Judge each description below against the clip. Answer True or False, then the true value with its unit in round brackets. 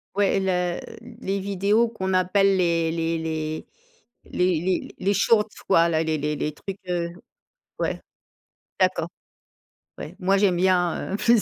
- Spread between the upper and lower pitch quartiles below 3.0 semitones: True (2.6 semitones)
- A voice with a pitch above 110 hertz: True (185 Hz)